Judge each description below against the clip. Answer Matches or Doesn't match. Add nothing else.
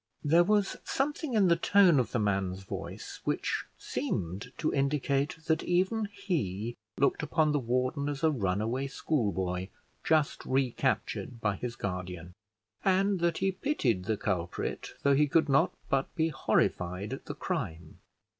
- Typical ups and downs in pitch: Doesn't match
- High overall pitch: Doesn't match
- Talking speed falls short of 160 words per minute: Matches